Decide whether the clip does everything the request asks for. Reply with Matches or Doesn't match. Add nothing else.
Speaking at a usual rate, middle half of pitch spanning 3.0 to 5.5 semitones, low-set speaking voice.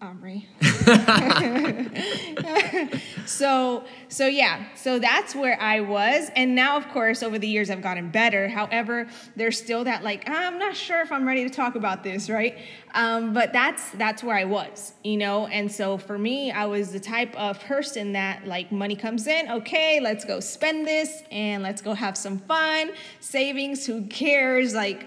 Doesn't match